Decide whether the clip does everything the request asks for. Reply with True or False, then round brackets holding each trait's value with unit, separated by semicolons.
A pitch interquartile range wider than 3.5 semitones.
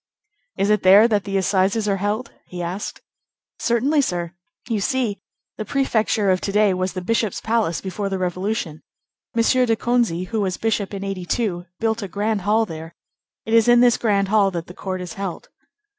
False (3.2 semitones)